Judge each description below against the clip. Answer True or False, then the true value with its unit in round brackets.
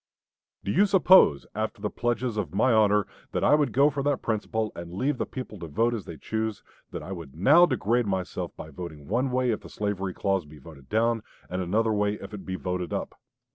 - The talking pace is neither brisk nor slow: False (220 wpm)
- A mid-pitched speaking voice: False (105 Hz)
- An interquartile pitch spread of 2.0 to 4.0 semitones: False (4.7 semitones)